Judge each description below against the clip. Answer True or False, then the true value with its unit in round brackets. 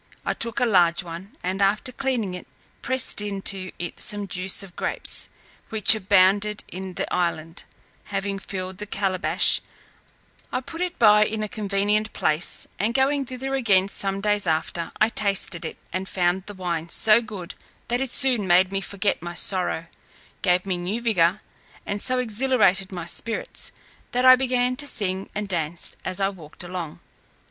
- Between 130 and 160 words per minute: False (170 wpm)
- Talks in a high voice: True (195 Hz)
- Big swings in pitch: False (3.3 semitones)